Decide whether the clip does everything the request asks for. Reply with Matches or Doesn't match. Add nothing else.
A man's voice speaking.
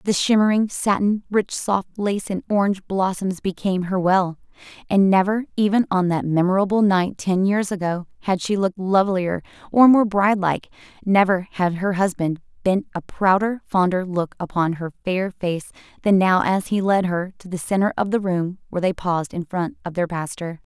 Doesn't match